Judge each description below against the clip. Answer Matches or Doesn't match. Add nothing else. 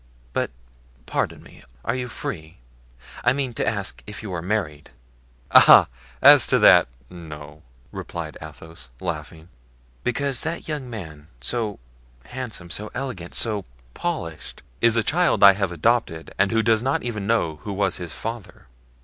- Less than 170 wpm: Matches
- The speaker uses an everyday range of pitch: Doesn't match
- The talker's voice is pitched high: Doesn't match